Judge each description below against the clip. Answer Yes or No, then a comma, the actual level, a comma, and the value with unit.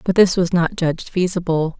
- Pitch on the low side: No, medium, 175 Hz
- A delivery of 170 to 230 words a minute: Yes, average, 200 wpm